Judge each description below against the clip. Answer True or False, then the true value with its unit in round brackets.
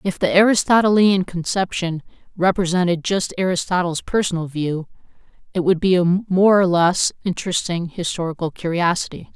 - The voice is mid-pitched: True (180 Hz)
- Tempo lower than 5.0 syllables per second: False (5.2 syllables/s)